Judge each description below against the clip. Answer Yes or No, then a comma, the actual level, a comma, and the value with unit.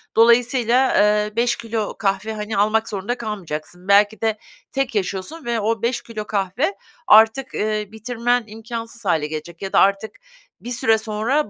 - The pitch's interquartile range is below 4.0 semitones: Yes, narrow, 2.4 semitones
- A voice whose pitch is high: Yes, high, 220 Hz